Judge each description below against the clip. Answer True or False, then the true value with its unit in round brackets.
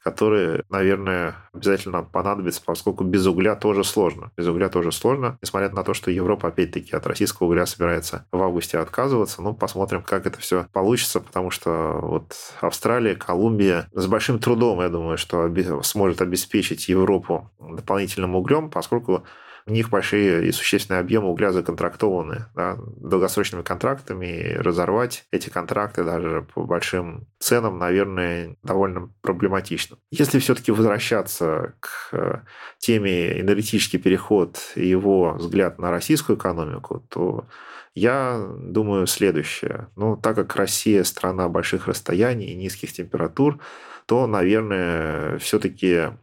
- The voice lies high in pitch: False (95 Hz)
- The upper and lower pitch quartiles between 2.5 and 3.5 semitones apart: True (3.2 semitones)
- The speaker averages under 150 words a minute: True (130 wpm)